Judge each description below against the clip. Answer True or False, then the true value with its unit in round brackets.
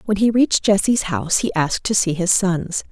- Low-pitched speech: False (190 Hz)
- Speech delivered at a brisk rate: True (225 wpm)